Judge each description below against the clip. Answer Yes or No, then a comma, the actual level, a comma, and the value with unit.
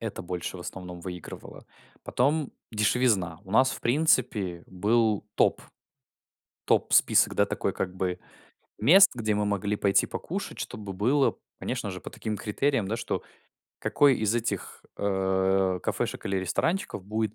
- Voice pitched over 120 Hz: No, low, 105 Hz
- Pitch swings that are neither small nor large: Yes, average, 4.0 semitones